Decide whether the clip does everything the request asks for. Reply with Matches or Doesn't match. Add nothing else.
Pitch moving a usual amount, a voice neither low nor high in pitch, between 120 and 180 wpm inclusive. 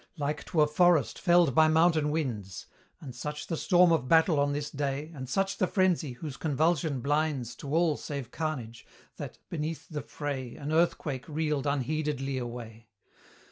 Matches